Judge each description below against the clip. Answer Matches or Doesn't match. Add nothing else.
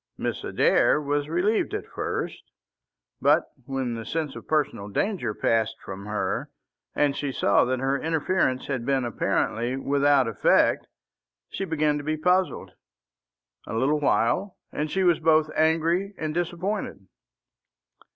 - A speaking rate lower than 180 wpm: Matches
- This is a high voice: Doesn't match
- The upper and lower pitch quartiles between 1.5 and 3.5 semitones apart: Doesn't match